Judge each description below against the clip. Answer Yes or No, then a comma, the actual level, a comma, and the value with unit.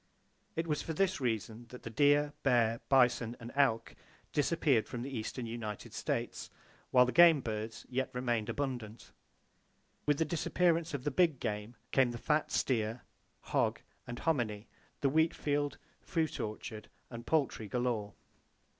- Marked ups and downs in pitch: No, average, 4.4 semitones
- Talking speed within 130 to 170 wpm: Yes, average, 150 wpm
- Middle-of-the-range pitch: No, low, 125 Hz